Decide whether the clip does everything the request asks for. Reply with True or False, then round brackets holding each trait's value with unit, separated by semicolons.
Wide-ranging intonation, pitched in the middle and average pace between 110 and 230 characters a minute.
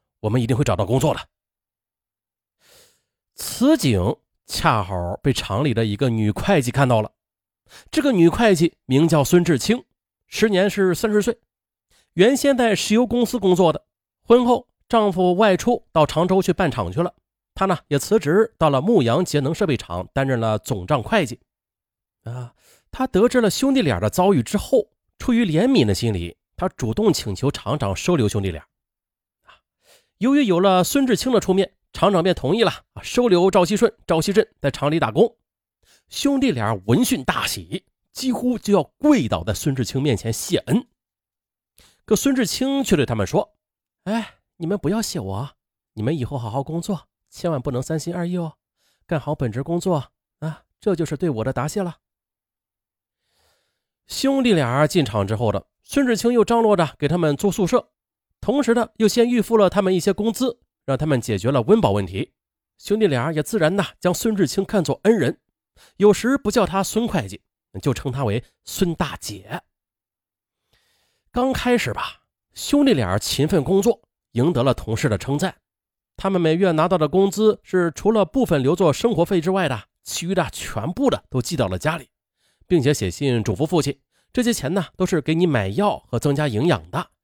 False (8.8 semitones; 170 Hz; 255 characters per minute)